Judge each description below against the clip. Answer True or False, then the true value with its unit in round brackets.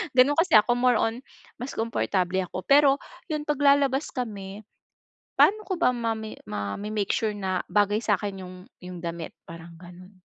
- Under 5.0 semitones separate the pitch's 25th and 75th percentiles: False (5.4 semitones)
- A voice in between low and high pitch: False (210 Hz)